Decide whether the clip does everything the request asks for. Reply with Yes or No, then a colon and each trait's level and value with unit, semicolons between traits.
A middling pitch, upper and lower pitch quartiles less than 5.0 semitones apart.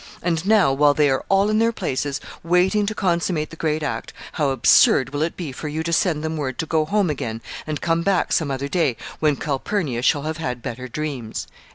Yes: medium, 155 Hz; average, 3.8 semitones